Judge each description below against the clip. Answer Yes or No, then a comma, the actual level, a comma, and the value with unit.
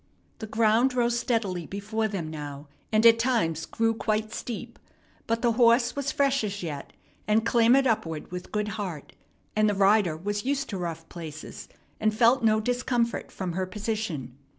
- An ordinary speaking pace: Yes, average, 170 wpm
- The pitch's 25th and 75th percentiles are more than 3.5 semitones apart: Yes, average, 4.2 semitones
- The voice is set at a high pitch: Yes, high, 215 Hz